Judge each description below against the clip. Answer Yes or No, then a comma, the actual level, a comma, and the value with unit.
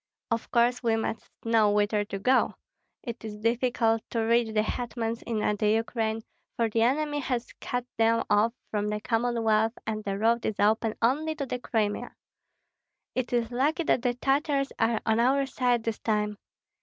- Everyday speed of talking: Yes, average, 175 wpm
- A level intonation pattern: Yes, narrow, 2.1 semitones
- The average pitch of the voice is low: No, high, 230 Hz